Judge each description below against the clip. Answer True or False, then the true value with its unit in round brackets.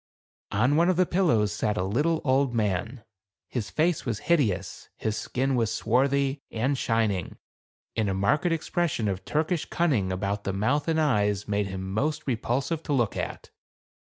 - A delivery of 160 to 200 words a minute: True (165 wpm)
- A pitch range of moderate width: False (6.3 semitones)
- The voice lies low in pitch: True (120 Hz)